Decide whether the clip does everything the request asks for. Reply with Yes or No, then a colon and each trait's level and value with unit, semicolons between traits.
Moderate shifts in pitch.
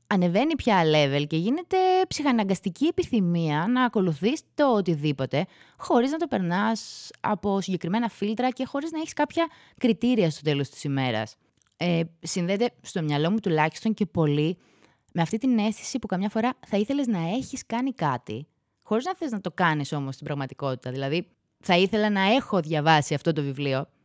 No: wide, 8.0 semitones